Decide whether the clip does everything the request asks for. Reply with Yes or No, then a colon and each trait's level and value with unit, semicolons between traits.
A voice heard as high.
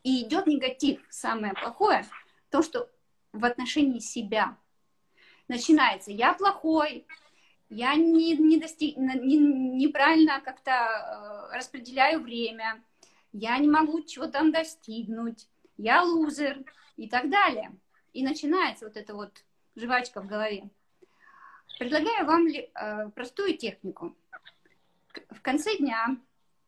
Yes: very high, 280 Hz